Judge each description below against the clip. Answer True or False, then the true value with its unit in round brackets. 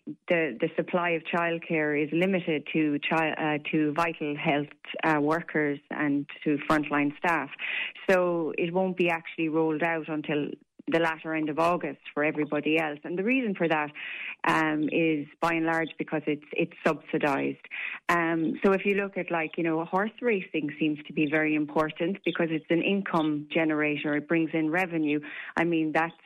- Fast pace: False (175 wpm)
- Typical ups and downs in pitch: False (2.1 semitones)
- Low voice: False (160 Hz)